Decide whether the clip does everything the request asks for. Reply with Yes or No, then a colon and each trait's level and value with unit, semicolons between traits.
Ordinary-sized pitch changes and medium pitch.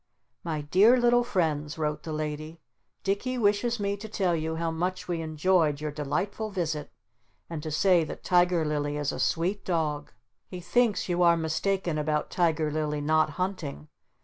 Yes: average, 3.8 semitones; medium, 165 Hz